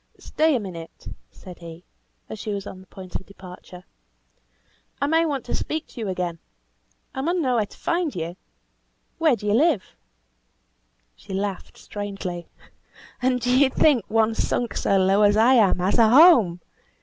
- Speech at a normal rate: Yes, average, 175 wpm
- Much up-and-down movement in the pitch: Yes, wide, 5.9 semitones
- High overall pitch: Yes, high, 210 Hz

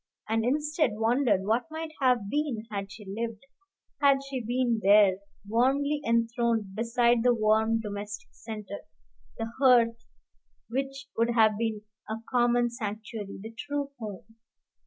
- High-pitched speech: Yes, high, 230 Hz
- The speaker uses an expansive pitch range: No, average, 2.8 semitones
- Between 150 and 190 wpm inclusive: No, slow, 135 wpm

